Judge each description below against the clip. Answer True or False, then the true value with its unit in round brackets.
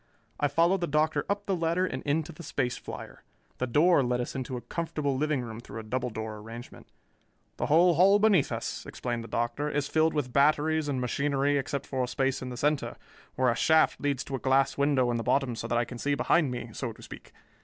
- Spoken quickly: True (230 wpm)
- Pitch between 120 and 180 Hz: True (140 Hz)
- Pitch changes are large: False (3.9 semitones)